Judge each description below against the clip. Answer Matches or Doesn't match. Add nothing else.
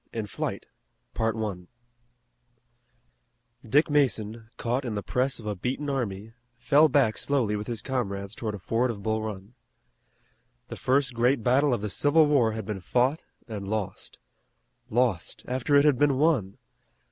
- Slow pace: Doesn't match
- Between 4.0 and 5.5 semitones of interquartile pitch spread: Matches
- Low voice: Matches